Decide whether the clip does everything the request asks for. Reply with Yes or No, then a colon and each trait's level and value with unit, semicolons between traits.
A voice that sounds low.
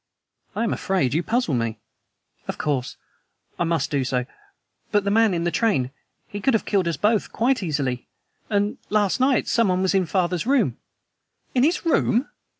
No: high, 195 Hz